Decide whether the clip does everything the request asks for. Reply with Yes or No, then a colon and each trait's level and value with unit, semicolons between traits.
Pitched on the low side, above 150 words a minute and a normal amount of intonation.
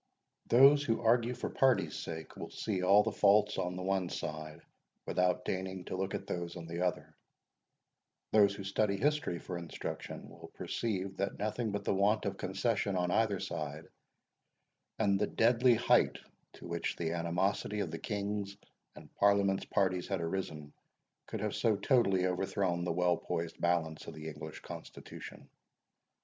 Yes: very low, 95 Hz; average, 160 wpm; average, 3.1 semitones